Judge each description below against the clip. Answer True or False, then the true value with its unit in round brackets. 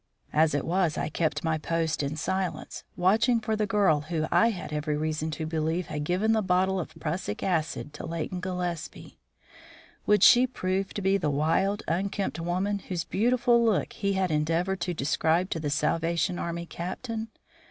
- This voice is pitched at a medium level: True (175 Hz)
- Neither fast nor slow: True (175 wpm)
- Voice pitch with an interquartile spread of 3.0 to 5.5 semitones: True (3.7 semitones)